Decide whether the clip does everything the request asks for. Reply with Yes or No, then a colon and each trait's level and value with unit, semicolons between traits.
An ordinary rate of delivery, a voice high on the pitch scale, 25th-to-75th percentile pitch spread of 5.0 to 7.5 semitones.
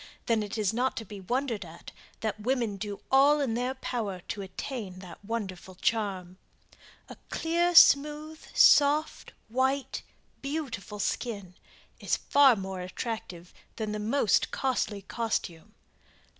No: slow, 130 wpm; high, 225 Hz; average, 5.3 semitones